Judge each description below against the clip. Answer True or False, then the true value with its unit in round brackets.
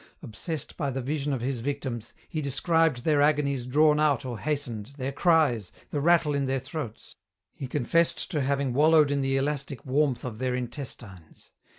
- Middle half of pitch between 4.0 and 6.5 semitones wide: False (3.0 semitones)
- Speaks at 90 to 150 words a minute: False (175 wpm)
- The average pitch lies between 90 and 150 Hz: True (140 Hz)